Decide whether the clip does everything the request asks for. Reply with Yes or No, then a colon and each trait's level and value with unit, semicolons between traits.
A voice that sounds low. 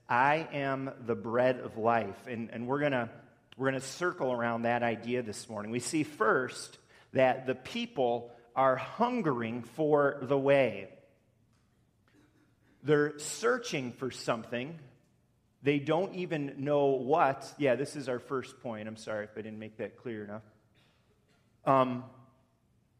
Yes: low, 130 Hz